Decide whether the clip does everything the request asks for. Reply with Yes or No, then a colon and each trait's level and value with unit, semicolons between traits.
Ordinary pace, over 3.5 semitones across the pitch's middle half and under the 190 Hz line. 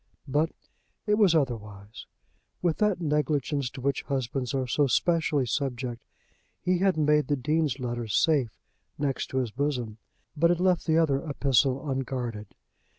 Yes: average, 150 wpm; average, 4.1 semitones; medium, 140 Hz